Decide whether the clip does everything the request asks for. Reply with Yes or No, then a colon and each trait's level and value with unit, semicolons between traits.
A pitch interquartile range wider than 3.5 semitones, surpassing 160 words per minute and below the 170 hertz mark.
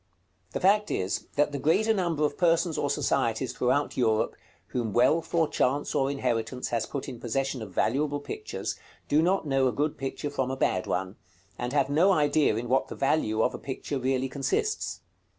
Yes: average, 3.9 semitones; average, 190 wpm; medium, 140 Hz